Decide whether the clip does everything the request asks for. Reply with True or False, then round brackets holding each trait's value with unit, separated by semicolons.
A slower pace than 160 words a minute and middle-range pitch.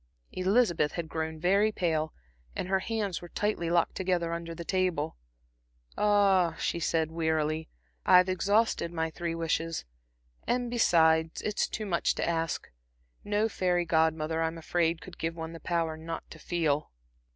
True (150 wpm; 170 Hz)